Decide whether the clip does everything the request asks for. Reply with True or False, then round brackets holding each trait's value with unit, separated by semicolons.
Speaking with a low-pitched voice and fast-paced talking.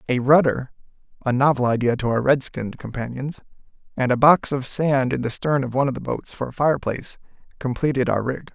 True (130 Hz; 210 wpm)